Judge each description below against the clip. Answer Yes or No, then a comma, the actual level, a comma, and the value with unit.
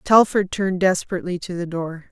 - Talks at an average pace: Yes, average, 170 wpm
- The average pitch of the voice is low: No, medium, 180 Hz